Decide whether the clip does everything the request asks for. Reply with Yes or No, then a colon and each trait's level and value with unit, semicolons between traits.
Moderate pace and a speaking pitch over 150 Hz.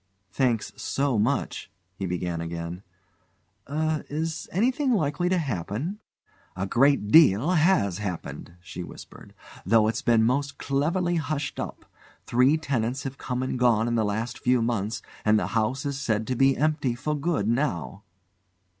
No: average, 155 wpm; low, 125 Hz